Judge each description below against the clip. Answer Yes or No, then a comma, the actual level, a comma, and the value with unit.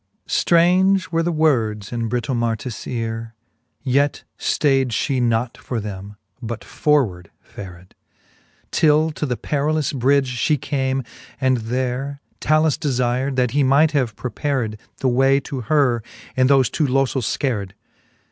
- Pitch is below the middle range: Yes, low, 130 Hz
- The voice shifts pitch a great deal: No, average, 3.6 semitones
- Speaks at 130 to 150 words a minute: Yes, average, 140 wpm